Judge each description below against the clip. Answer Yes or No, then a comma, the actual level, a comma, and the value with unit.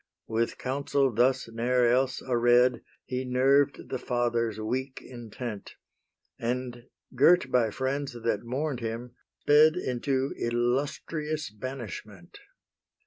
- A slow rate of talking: Yes, slow, 105 wpm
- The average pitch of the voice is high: No, low, 125 Hz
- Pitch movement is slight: Yes, narrow, 2.2 semitones